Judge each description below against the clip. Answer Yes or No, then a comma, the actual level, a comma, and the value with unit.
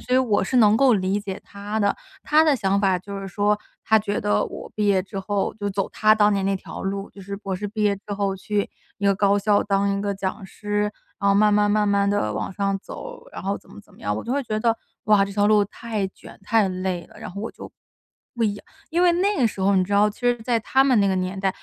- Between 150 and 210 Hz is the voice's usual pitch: Yes, high, 205 Hz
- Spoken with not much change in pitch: Yes, narrow, 1.6 semitones